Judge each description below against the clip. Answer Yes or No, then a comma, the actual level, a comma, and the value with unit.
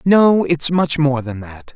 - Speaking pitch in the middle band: Yes, medium, 150 Hz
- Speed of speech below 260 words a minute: Yes, fast, 205 wpm